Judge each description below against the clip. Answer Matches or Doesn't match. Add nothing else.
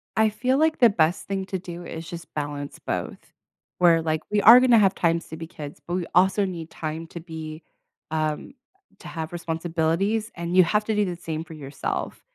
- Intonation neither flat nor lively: Matches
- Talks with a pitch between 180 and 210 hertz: Doesn't match